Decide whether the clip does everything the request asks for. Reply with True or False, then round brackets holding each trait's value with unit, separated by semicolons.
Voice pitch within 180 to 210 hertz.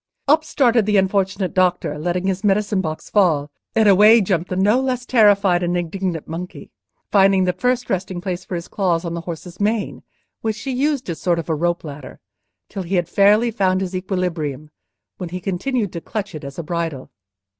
True (185 Hz)